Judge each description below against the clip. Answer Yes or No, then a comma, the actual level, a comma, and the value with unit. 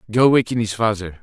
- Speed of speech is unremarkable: Yes, average, 195 wpm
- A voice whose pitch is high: No, low, 110 Hz